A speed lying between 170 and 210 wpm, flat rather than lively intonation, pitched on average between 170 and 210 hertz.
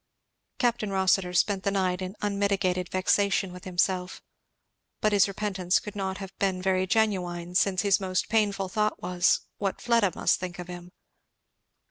No: average, 155 wpm; narrow, 1.8 semitones; high, 190 Hz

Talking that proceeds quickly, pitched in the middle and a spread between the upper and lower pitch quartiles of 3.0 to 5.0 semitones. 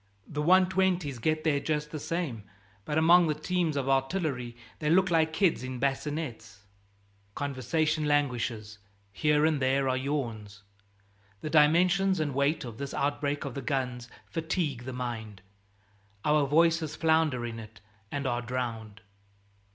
No: average, 145 wpm; medium, 145 Hz; average, 4.2 semitones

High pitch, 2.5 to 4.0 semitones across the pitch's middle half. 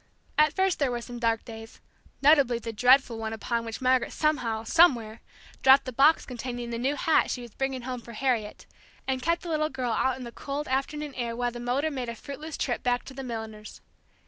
Yes: very high, 250 Hz; average, 3.0 semitones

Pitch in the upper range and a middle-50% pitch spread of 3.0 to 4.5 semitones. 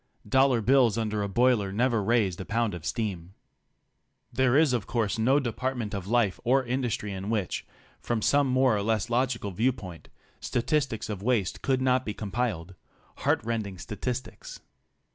No: low, 115 Hz; average, 3.8 semitones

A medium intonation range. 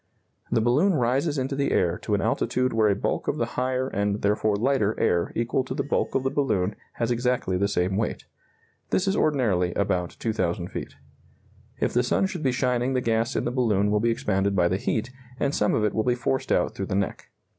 Yes: average, 4.4 semitones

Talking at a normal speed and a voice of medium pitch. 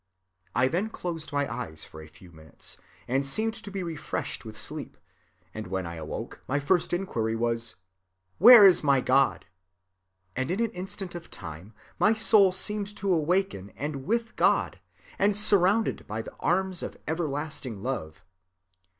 Yes: average, 160 wpm; medium, 155 Hz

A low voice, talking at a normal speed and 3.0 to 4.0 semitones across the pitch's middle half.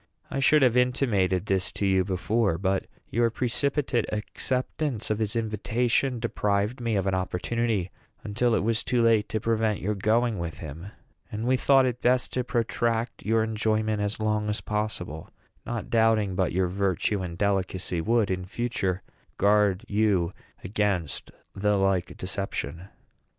Yes: low, 105 Hz; average, 155 wpm; average, 3.4 semitones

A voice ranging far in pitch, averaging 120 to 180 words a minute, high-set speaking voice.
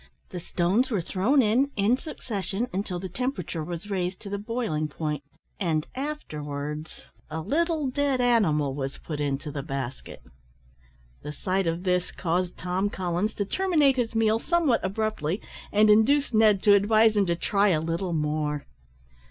Yes: wide, 5.9 semitones; average, 160 wpm; high, 195 Hz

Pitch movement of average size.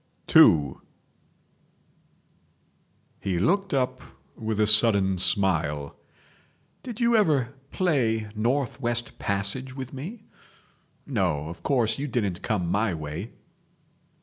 No: wide, 5.8 semitones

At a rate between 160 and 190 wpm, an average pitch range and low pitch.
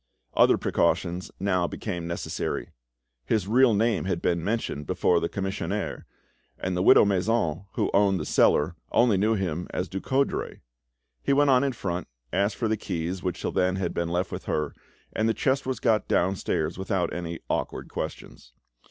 Yes: average, 170 wpm; average, 4.1 semitones; very low, 95 Hz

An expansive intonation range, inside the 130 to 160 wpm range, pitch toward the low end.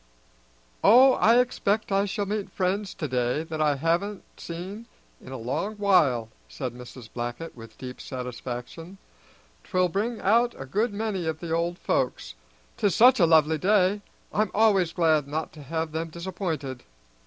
No: wide, 6.2 semitones; average, 155 wpm; medium, 170 Hz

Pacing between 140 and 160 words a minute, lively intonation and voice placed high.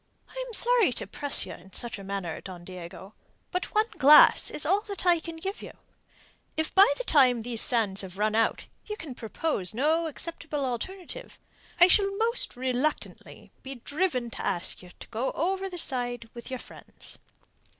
No: average, 180 wpm; wide, 8.3 semitones; very high, 270 Hz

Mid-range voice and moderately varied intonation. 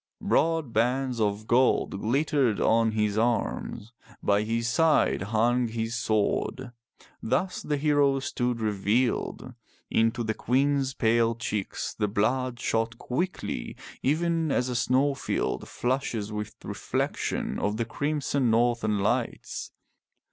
No: low, 120 Hz; average, 3.4 semitones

